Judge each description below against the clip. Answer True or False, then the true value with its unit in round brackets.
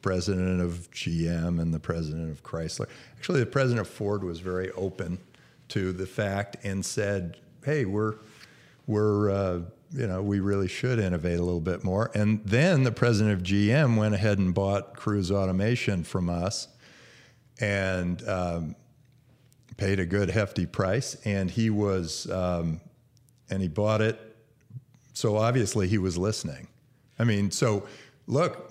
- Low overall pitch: True (100 Hz)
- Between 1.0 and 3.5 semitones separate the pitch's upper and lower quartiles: False (4.1 semitones)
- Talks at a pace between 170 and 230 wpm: False (155 wpm)